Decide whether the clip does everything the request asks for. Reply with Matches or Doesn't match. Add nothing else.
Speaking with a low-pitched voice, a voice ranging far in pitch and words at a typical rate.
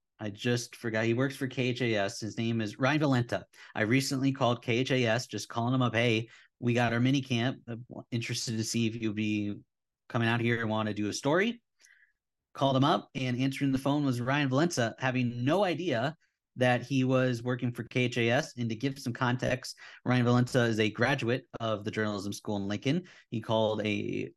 Doesn't match